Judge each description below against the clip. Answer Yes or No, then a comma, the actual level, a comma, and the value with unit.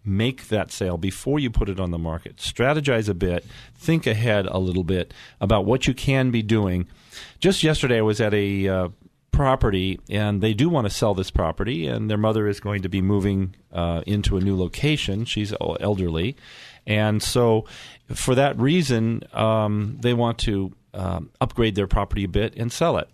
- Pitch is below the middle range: Yes, low, 105 Hz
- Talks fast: No, average, 190 wpm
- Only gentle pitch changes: No, average, 3.6 semitones